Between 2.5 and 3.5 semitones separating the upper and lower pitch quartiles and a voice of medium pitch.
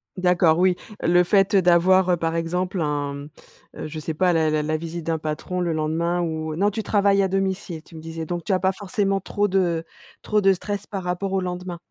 Yes: average, 2.9 semitones; medium, 175 Hz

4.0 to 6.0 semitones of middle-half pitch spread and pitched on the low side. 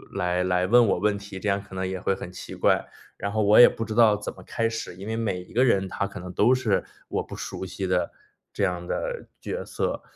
No: average, 3.5 semitones; low, 100 Hz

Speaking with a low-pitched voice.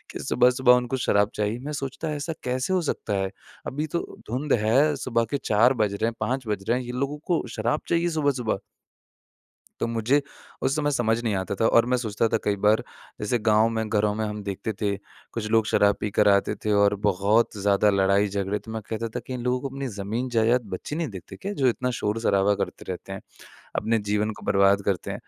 Yes: low, 115 Hz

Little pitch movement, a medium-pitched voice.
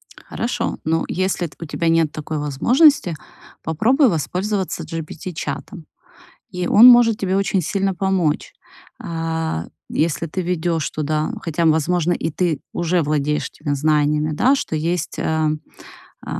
No: average, 3.5 semitones; medium, 165 Hz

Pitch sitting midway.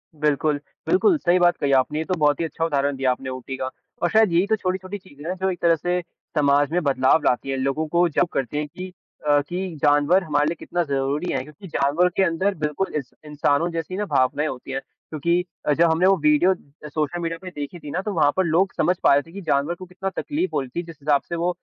Yes: medium, 160 Hz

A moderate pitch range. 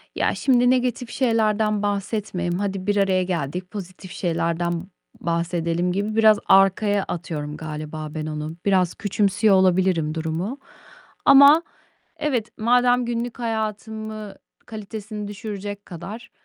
Yes: average, 4.0 semitones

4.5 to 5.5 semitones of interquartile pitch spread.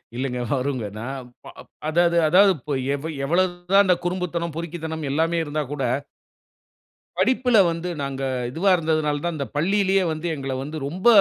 No: average, 3.8 semitones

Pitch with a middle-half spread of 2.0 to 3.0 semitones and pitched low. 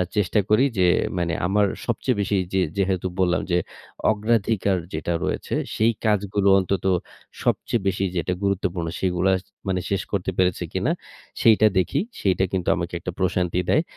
Yes: narrow, 2.4 semitones; very low, 95 Hz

